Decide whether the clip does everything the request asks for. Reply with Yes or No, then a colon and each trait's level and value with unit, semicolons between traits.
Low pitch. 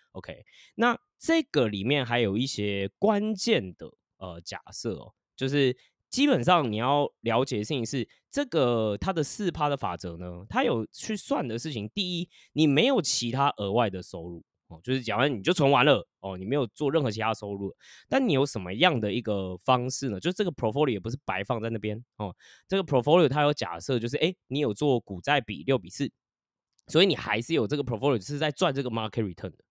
Yes: low, 130 Hz